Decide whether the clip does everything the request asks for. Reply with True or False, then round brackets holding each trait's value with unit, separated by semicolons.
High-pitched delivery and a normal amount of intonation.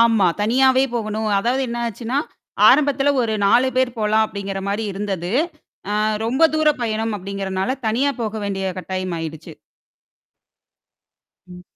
True (220 Hz; 4.2 semitones)